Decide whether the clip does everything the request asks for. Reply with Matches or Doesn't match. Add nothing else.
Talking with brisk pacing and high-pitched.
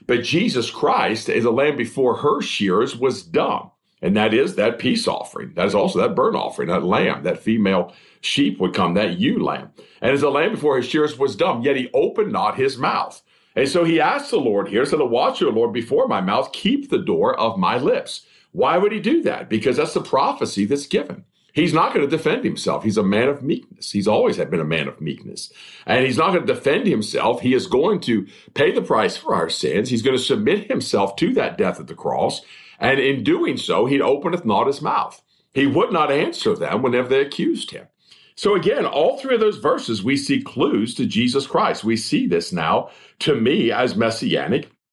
Matches